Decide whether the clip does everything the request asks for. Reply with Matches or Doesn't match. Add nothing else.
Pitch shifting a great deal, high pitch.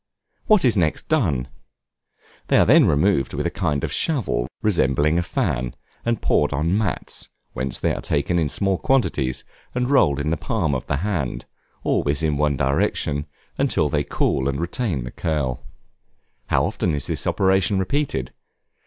Doesn't match